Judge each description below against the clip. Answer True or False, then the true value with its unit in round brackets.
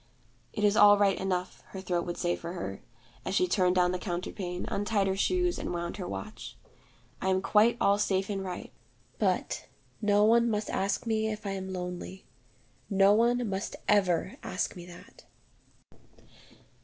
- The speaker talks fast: False (170 wpm)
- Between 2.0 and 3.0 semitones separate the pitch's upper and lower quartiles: True (2.6 semitones)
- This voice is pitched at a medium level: False (195 Hz)